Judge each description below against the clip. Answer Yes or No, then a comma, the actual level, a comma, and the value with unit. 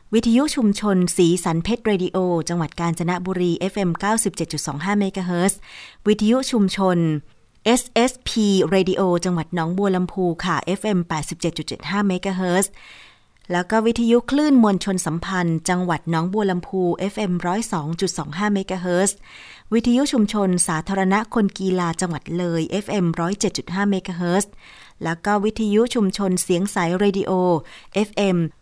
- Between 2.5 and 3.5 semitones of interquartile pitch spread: Yes, average, 2.9 semitones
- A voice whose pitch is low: No, medium, 185 Hz